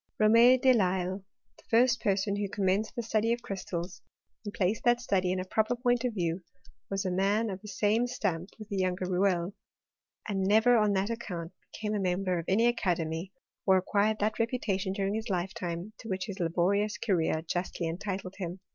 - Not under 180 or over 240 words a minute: Yes, average, 190 wpm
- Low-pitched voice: No, high, 195 Hz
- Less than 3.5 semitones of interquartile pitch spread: Yes, average, 3.0 semitones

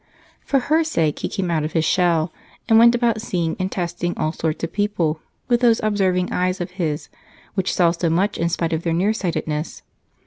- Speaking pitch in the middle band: Yes, medium, 180 Hz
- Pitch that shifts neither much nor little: Yes, average, 4.0 semitones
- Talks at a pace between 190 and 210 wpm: Yes, average, 200 wpm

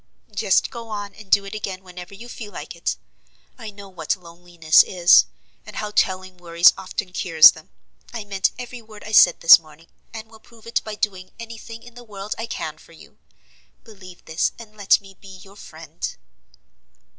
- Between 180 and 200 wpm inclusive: Yes, average, 190 wpm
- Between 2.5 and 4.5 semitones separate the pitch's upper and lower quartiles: Yes, average, 3.3 semitones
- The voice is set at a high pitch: Yes, high, 195 Hz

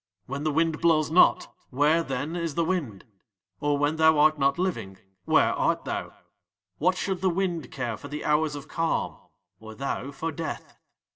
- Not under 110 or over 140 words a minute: No, average, 180 wpm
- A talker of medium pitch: Yes, medium, 155 Hz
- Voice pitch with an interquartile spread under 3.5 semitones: Yes, average, 2.8 semitones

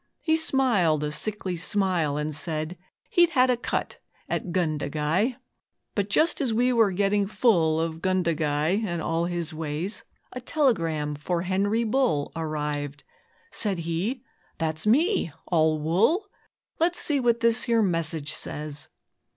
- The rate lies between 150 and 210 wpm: No, average, 140 wpm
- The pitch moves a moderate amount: No, wide, 6.6 semitones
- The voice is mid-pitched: Yes, medium, 180 Hz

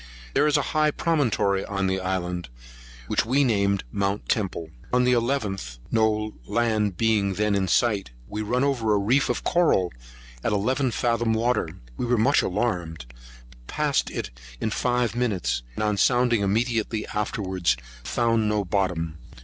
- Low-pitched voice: Yes, low, 105 Hz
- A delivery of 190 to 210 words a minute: No, average, 155 wpm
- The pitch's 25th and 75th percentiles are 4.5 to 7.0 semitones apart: No, average, 4.0 semitones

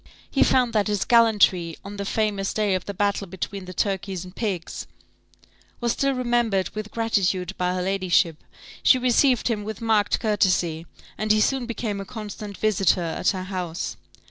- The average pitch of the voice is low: No, high, 205 Hz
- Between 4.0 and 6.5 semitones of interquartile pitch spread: No, average, 3.2 semitones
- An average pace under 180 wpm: Yes, average, 170 wpm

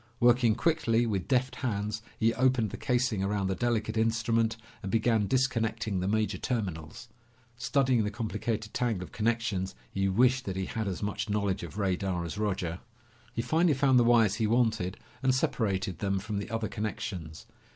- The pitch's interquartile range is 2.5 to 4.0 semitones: Yes, average, 3.5 semitones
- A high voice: No, low, 110 Hz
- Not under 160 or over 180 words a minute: Yes, average, 170 wpm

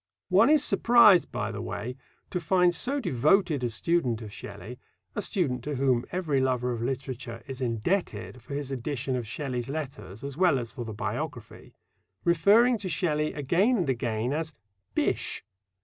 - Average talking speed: Yes, average, 165 wpm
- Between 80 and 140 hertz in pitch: Yes, low, 135 Hz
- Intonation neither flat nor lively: No, wide, 6.6 semitones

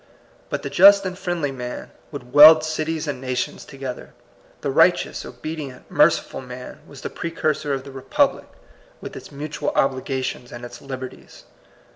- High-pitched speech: No, medium, 140 Hz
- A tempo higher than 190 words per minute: No, average, 160 wpm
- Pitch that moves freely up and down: No, average, 3.3 semitones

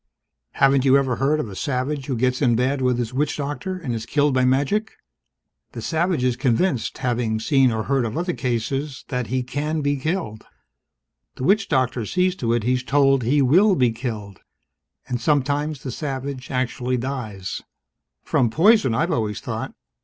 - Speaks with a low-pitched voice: Yes, low, 130 Hz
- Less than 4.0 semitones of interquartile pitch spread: Yes, average, 3.1 semitones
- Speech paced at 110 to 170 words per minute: No, average, 180 wpm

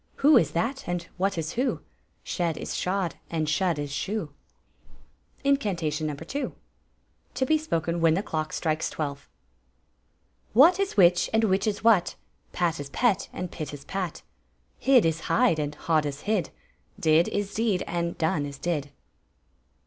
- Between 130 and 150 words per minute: No, average, 165 wpm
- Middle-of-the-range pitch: Yes, medium, 175 Hz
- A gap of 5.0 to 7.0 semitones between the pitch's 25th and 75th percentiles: Yes, average, 5.3 semitones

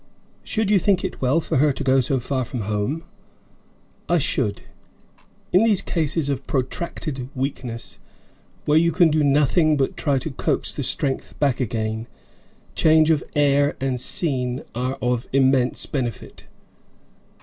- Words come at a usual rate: Yes, average, 150 wpm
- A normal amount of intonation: Yes, average, 3.7 semitones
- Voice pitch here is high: No, low, 135 Hz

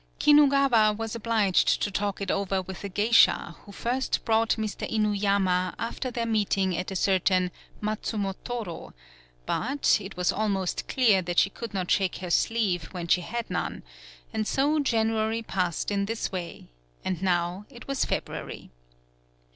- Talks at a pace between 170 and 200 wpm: No, average, 155 wpm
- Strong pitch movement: No, average, 3.5 semitones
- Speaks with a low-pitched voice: No, high, 205 Hz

